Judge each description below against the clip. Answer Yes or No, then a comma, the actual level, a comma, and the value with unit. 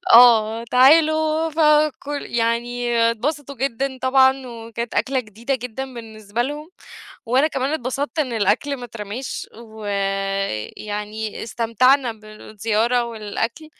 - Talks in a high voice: Yes, high, 240 Hz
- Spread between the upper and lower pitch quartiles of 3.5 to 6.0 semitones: Yes, average, 3.8 semitones